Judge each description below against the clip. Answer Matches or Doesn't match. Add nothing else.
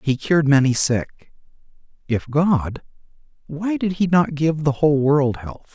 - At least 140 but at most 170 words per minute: Matches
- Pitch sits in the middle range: Matches